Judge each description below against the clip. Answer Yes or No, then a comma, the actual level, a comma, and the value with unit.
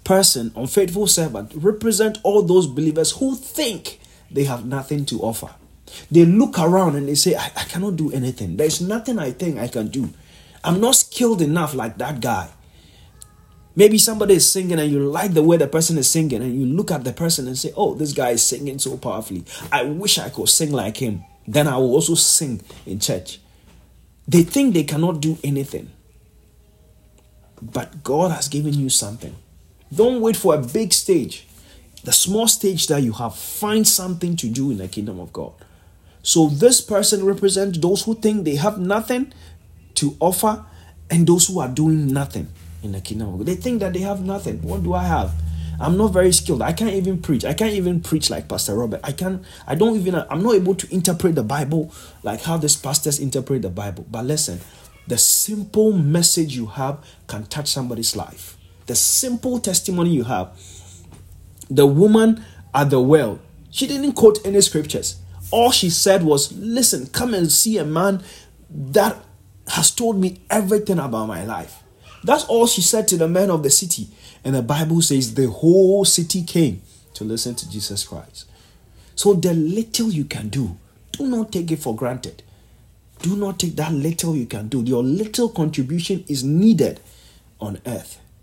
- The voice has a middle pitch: Yes, medium, 150 Hz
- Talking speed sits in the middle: Yes, average, 185 wpm